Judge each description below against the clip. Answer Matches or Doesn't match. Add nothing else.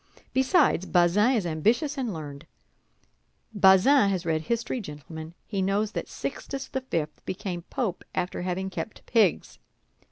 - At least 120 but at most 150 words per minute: Matches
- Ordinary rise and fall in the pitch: Doesn't match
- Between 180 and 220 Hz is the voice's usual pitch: Matches